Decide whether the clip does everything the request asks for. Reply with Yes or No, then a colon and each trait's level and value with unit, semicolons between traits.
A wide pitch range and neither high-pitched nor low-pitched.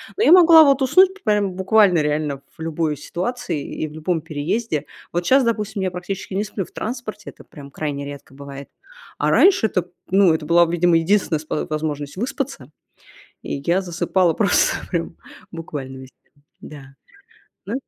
Yes: wide, 5.9 semitones; medium, 175 Hz